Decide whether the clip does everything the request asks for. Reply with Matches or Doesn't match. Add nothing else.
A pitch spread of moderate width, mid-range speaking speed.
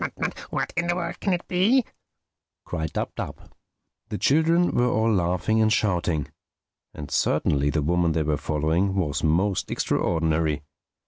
Doesn't match